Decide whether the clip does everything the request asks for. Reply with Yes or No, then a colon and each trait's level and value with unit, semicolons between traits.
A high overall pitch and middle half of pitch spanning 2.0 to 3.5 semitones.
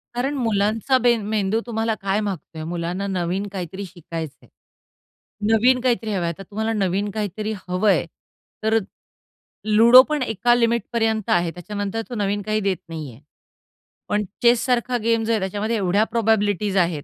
Yes: high, 210 Hz; average, 3.1 semitones